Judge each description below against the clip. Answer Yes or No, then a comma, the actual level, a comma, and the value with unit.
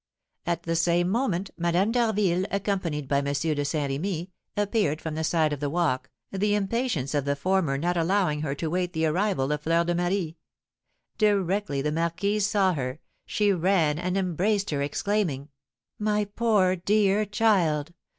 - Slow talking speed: No, average, 165 wpm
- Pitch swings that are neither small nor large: Yes, average, 4.8 semitones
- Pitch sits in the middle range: Yes, medium, 175 Hz